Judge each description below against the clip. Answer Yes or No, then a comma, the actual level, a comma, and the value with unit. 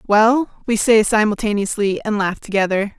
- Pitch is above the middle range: Yes, high, 210 Hz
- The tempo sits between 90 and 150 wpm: Yes, average, 140 wpm